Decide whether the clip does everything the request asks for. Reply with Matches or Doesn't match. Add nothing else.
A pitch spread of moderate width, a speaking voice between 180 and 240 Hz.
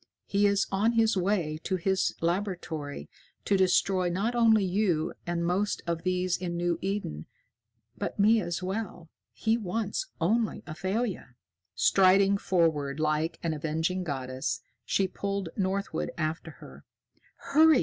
Matches